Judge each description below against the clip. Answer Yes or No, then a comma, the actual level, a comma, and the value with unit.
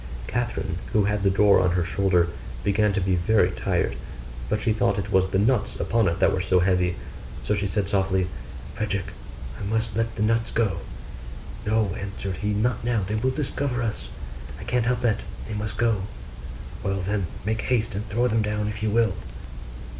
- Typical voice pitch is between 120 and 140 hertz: No, low, 105 Hz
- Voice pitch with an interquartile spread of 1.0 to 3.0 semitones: Yes, average, 2.7 semitones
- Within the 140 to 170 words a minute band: No, average, 190 wpm